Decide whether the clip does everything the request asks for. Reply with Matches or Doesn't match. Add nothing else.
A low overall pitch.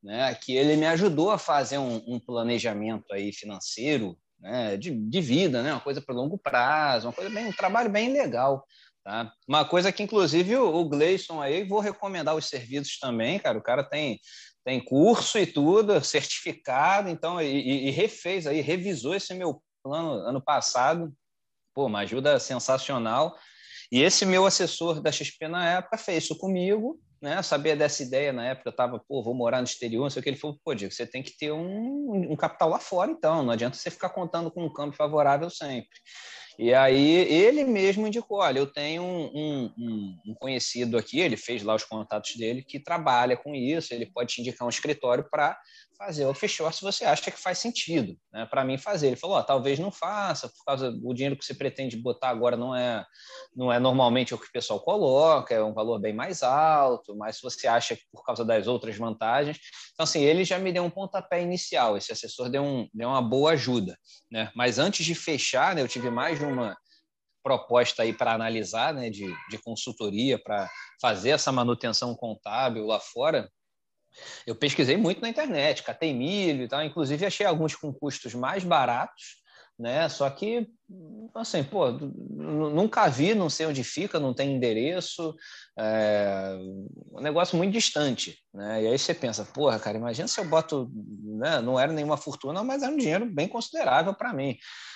Doesn't match